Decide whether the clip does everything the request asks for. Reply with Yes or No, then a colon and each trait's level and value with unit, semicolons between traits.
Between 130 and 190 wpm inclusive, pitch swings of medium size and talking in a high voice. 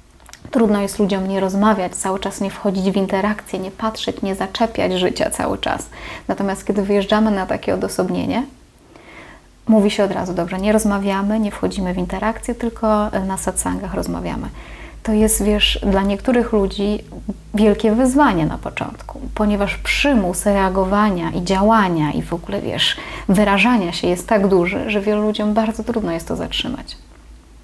No: average, 155 wpm; narrow, 2.3 semitones; high, 205 Hz